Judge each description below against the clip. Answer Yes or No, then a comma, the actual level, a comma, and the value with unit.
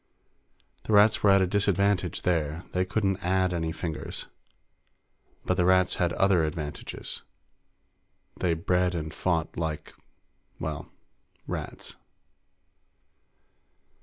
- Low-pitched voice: Yes, very low, 90 Hz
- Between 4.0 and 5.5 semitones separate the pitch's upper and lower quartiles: No, average, 2.9 semitones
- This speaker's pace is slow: Yes, slow, 110 wpm